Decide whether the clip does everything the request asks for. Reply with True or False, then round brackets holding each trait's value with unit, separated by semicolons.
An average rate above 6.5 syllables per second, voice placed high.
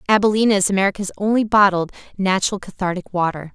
True (6.8 syllables/s; 195 Hz)